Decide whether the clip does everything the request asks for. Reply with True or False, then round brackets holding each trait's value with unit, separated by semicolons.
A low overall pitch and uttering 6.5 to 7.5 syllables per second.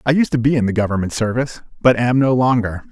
True (120 Hz; 6.6 syllables/s)